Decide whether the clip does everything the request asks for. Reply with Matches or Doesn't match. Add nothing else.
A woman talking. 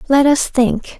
Matches